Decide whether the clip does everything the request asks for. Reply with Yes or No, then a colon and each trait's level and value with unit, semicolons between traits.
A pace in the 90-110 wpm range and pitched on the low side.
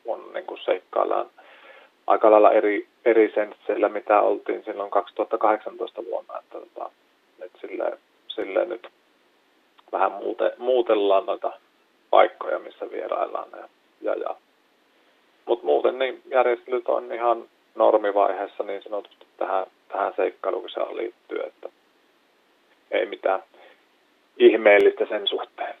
No: average, 105 wpm; very high, 380 Hz